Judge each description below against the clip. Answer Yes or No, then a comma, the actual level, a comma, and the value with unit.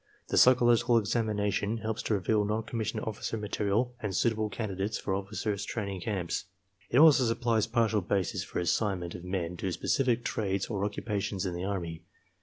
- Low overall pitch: Yes, low, 105 Hz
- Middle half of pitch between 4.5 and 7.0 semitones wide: No, average, 2.9 semitones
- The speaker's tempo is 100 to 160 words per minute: No, average, 175 wpm